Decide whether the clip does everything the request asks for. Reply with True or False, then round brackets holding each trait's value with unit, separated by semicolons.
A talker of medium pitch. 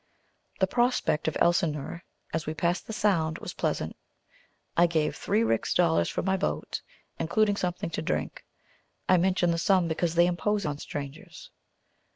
True (170 Hz)